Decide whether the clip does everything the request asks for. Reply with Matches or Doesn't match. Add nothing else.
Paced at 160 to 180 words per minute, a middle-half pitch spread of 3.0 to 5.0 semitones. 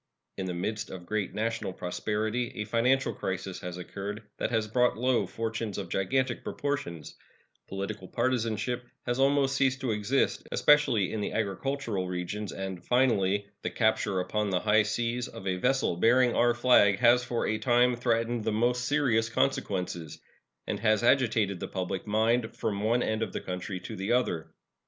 Matches